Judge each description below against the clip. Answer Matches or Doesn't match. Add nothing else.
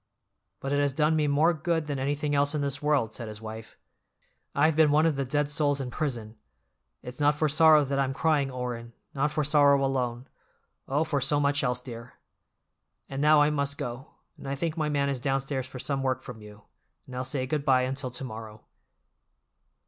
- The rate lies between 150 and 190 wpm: Doesn't match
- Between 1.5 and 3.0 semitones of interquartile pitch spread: Matches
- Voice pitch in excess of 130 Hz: Matches